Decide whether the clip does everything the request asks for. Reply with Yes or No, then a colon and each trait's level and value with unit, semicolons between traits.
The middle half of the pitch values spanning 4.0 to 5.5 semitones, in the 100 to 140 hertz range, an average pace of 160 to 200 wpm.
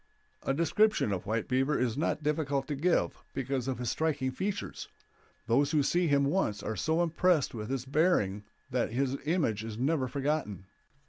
Yes: average, 4.7 semitones; low, 135 Hz; average, 175 wpm